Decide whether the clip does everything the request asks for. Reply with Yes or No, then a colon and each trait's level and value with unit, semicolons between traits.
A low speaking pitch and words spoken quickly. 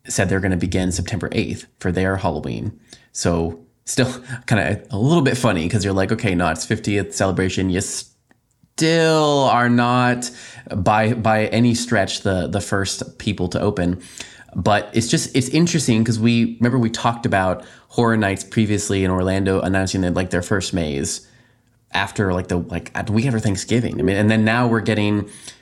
No: low, 105 Hz; average, 185 wpm